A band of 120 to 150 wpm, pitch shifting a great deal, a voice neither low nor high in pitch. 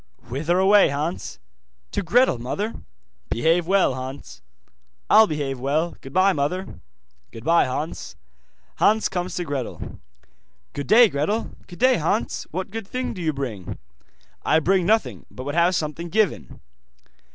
Yes: average, 140 wpm; wide, 5.7 semitones; medium, 170 Hz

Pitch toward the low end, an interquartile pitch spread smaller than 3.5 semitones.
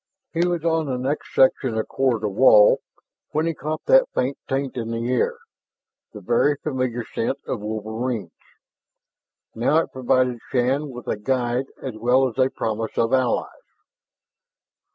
Yes: low, 125 Hz; average, 2.9 semitones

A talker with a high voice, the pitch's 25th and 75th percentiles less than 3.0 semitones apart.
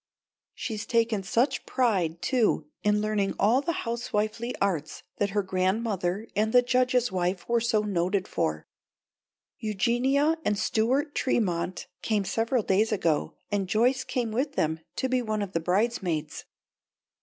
No: high, 215 Hz; average, 4.2 semitones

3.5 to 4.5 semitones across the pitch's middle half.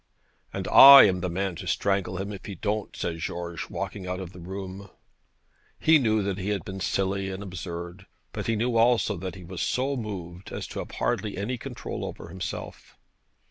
No: average, 2.7 semitones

